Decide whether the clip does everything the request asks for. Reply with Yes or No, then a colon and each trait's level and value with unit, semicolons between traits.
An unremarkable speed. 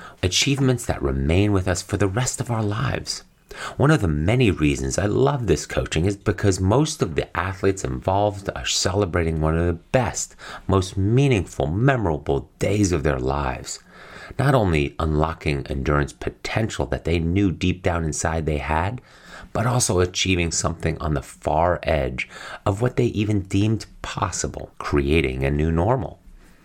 Yes: average, 160 wpm